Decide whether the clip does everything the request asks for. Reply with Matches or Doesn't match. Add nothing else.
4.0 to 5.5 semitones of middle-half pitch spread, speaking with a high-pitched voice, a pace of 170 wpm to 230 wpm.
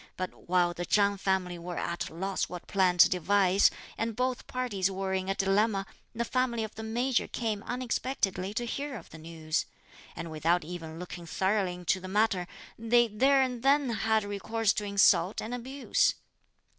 Matches